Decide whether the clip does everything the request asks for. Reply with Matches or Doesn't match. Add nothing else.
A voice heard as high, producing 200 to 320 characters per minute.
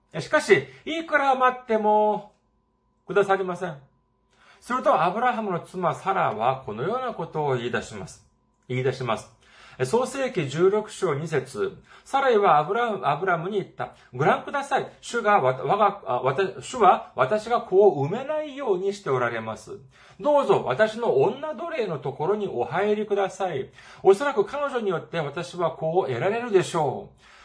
Matches